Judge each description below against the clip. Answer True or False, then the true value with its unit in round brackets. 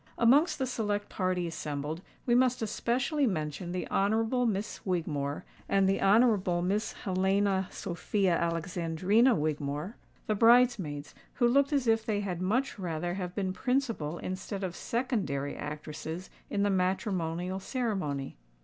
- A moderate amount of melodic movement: True (5.0 semitones)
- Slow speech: True (130 wpm)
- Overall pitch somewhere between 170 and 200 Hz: True (190 Hz)